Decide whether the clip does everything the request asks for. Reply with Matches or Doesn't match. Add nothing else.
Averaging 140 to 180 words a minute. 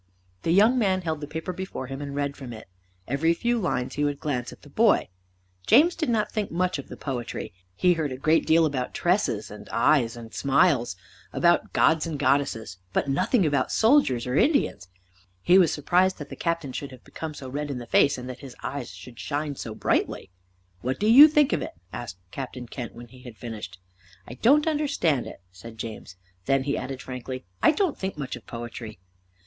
Doesn't match